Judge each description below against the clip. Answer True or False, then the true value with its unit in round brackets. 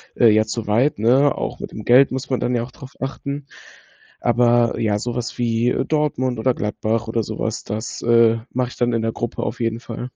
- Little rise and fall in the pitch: True (2.0 semitones)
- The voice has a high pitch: False (120 Hz)